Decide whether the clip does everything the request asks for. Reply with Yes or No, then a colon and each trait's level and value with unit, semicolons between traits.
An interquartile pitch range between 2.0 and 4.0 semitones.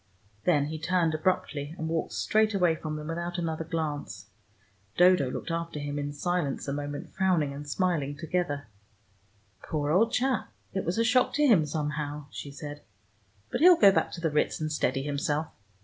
Yes: average, 3.6 semitones